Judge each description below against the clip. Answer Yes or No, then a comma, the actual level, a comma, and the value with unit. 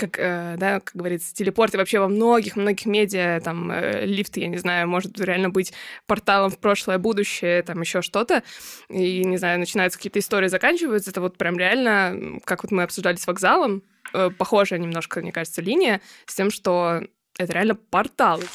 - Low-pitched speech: No, high, 190 Hz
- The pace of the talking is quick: Yes, fast, 175 wpm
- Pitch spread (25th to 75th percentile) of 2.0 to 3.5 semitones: Yes, narrow, 2.4 semitones